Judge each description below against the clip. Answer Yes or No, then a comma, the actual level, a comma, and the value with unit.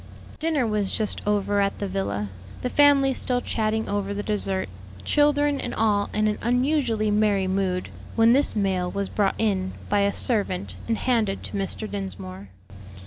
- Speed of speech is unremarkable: Yes, average, 165 wpm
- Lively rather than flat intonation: No, average, 3.2 semitones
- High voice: Yes, high, 210 Hz